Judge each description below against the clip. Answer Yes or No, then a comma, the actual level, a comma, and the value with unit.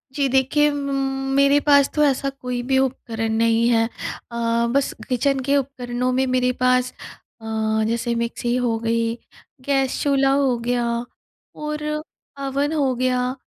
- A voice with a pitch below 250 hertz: No, very high, 255 Hz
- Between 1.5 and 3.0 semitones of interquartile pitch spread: Yes, narrow, 2.4 semitones